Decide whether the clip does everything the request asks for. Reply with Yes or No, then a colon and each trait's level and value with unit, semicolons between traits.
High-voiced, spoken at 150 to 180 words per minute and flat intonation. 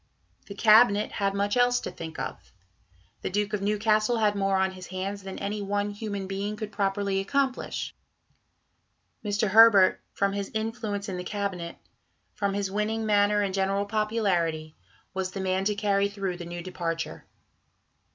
Yes: high, 200 Hz; average, 160 wpm; narrow, 1.7 semitones